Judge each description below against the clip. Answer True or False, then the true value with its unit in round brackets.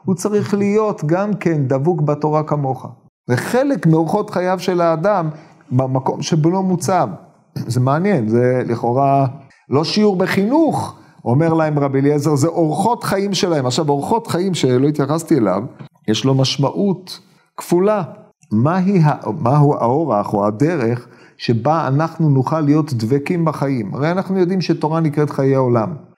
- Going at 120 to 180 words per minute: True (140 wpm)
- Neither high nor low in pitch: True (155 Hz)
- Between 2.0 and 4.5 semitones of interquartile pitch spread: False (5.2 semitones)